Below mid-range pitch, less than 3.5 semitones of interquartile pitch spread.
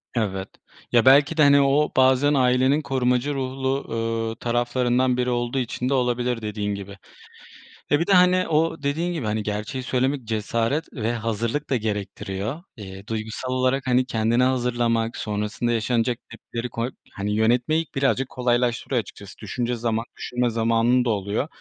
Yes: low, 125 Hz; average, 2.8 semitones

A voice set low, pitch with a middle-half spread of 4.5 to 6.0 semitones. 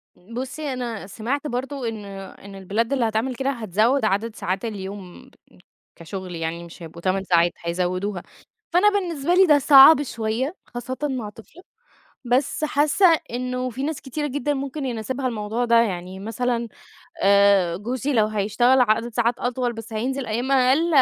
No: high, 235 Hz; average, 4.9 semitones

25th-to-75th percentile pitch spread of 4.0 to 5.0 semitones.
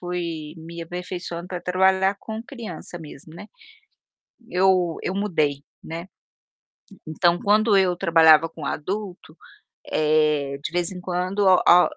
No: average, 2.8 semitones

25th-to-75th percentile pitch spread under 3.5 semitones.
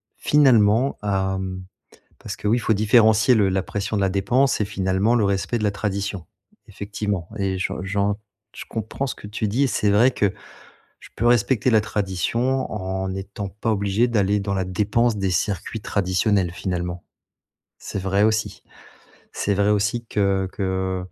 Yes: narrow, 2.4 semitones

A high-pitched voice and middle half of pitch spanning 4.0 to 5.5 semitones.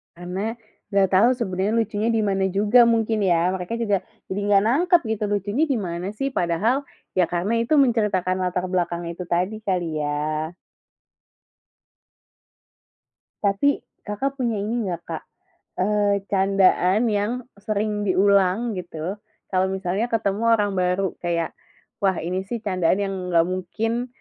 No: high, 195 Hz; average, 3.3 semitones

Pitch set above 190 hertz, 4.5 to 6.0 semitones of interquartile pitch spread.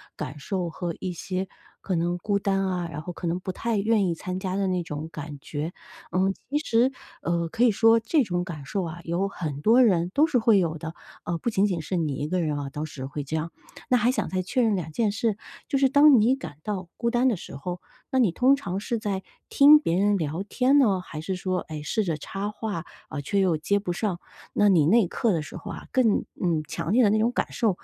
No: medium, 185 Hz; average, 5.0 semitones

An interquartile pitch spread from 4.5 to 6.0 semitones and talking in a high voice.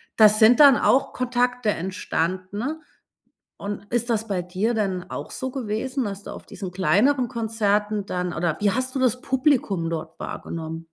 Yes: average, 5.0 semitones; high, 215 Hz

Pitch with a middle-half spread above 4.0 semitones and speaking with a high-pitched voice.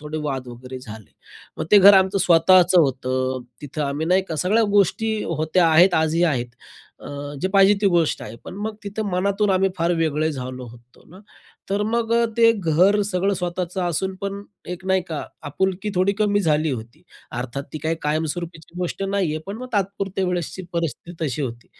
No: average, 4.6 semitones; medium, 175 Hz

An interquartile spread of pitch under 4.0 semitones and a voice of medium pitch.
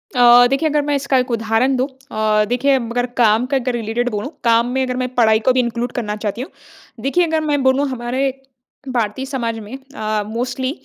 No: average, 2.8 semitones; high, 245 Hz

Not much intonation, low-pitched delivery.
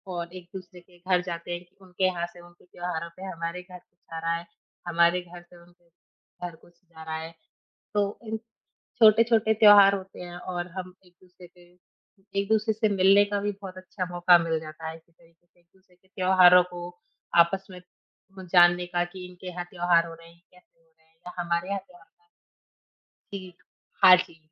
No: narrow, 1.4 semitones; medium, 180 Hz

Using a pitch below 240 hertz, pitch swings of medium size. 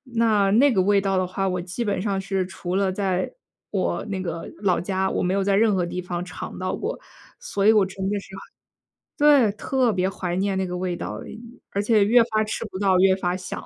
No: high, 195 Hz; narrow, 2.0 semitones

